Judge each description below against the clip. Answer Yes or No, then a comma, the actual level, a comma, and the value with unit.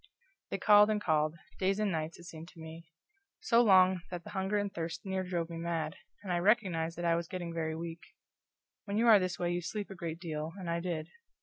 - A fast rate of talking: Yes, fast, 230 wpm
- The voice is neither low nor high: Yes, medium, 175 Hz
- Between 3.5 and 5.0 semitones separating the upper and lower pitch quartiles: No, average, 2.7 semitones